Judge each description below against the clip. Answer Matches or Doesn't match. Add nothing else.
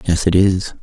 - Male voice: Matches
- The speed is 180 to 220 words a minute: Matches